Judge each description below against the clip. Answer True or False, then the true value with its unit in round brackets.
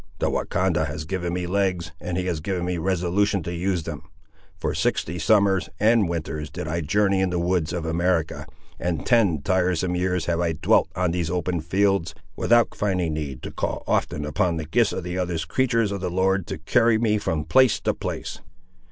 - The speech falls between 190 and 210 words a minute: True (195 wpm)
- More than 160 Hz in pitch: False (90 Hz)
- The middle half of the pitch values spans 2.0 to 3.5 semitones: True (2.8 semitones)